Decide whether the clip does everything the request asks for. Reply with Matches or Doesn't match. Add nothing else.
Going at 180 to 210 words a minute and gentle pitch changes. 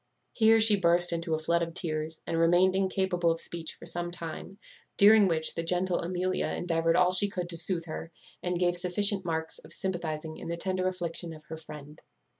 Matches